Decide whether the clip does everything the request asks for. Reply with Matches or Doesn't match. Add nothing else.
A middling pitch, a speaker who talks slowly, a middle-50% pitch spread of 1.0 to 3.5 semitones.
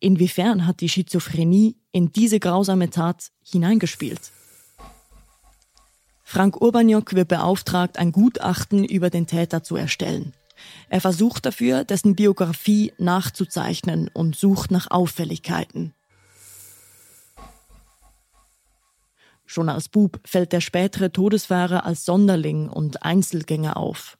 Matches